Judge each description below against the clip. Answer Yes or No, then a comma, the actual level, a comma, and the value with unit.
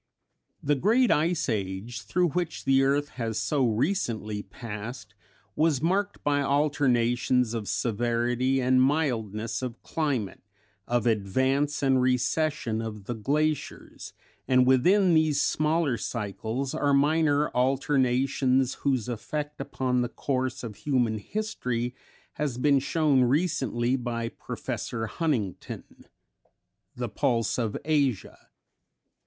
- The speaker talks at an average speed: No, slow, 115 wpm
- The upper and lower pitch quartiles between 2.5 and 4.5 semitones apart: Yes, average, 4.0 semitones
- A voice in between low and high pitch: No, low, 130 Hz